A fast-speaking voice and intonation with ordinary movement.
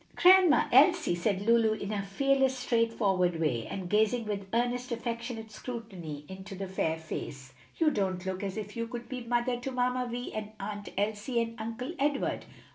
No: average, 175 wpm; average, 4.0 semitones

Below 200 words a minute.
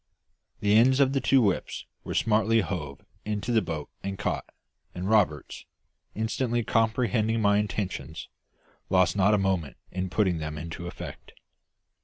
Yes: average, 145 wpm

